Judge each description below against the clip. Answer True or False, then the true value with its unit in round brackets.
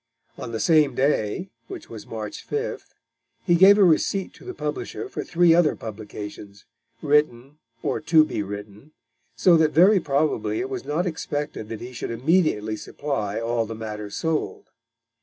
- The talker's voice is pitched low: False (150 Hz)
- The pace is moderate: True (160 wpm)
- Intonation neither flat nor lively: False (7.7 semitones)